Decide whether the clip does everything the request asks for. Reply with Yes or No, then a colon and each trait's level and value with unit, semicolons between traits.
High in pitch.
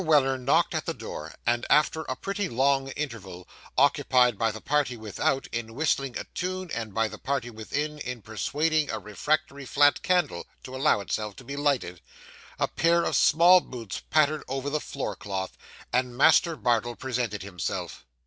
No: low, 130 Hz